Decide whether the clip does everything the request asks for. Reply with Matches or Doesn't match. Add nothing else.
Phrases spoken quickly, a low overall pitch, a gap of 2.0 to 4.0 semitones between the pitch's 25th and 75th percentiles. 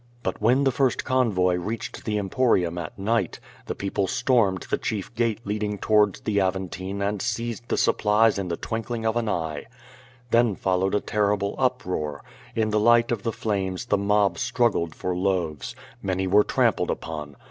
Doesn't match